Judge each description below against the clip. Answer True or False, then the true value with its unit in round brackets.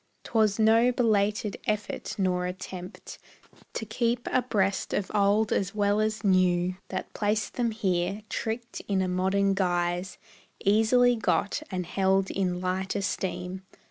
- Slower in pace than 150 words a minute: True (140 wpm)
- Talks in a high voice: True (200 Hz)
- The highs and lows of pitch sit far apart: False (2.8 semitones)